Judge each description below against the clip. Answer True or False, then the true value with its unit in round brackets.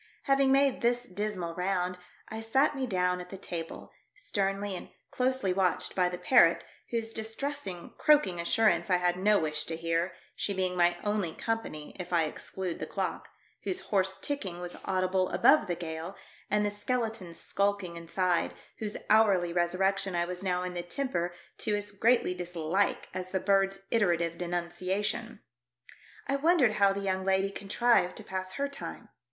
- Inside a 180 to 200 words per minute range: False (170 wpm)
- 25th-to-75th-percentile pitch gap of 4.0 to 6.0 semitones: False (3.6 semitones)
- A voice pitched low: False (190 Hz)